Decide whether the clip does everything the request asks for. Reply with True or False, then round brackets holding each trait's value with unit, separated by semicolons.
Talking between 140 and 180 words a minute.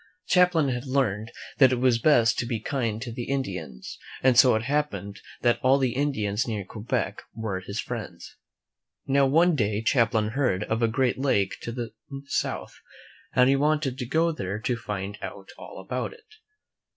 True (175 wpm)